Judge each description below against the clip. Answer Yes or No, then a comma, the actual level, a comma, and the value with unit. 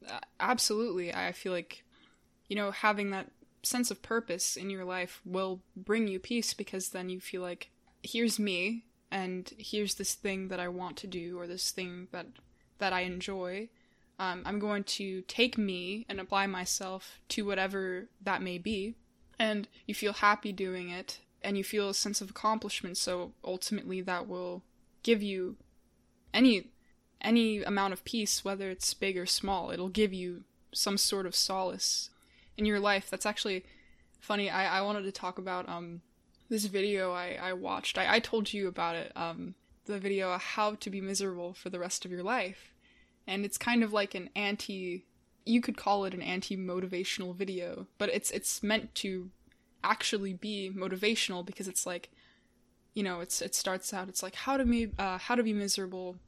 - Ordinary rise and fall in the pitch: No, narrow, 2.3 semitones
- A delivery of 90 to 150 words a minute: No, average, 180 wpm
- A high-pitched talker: Yes, high, 195 Hz